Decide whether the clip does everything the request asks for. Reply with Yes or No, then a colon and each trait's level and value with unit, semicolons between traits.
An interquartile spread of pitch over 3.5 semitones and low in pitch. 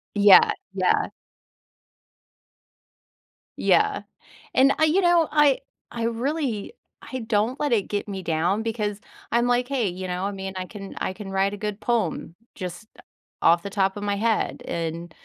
No: average, 4.0 semitones; high, 210 Hz